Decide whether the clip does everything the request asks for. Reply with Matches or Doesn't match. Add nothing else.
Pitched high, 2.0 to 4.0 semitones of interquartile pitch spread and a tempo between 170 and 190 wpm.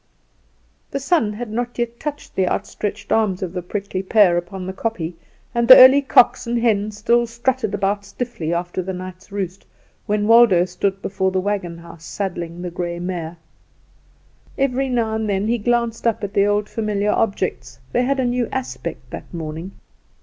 Doesn't match